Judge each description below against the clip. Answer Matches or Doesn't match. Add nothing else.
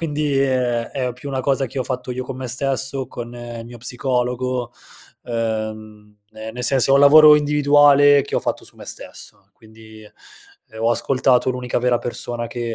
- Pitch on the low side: Matches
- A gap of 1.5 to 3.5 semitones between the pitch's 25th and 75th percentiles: Matches